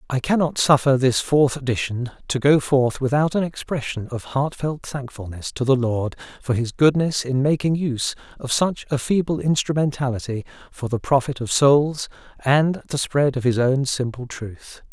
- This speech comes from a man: Yes, male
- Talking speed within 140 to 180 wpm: Yes, average, 170 wpm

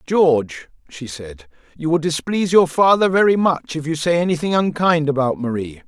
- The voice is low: No, medium, 155 Hz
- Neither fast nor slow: Yes, average, 175 wpm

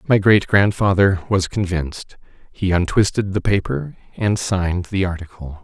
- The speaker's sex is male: Yes, male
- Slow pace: Yes, slow, 130 wpm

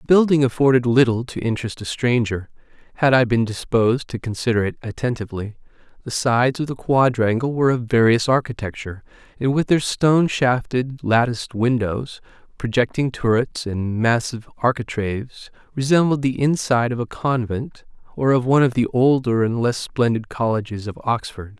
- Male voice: Yes, male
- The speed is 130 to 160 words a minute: Yes, average, 155 wpm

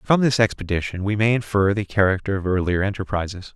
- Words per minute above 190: Yes, average, 200 wpm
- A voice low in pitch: Yes, low, 100 Hz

